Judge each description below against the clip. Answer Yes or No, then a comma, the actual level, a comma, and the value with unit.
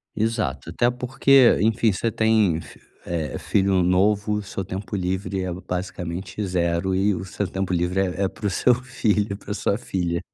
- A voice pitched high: No, very low, 95 Hz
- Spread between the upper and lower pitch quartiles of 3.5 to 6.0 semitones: No, average, 2.9 semitones